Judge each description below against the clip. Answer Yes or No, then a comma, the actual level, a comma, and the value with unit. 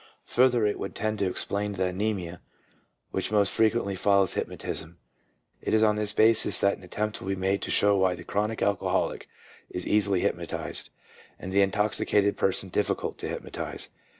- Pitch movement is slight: Yes, narrow, 1.9 semitones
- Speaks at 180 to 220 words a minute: No, average, 170 wpm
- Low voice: Yes, low, 100 Hz